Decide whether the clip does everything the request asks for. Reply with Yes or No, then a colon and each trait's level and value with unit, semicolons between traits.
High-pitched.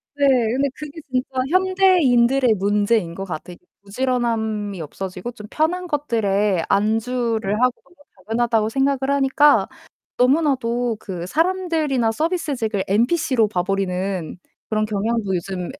Yes: high, 230 Hz